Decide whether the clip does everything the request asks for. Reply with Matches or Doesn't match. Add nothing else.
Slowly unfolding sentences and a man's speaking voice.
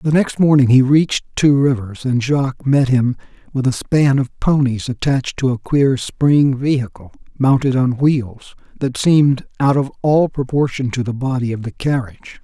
Doesn't match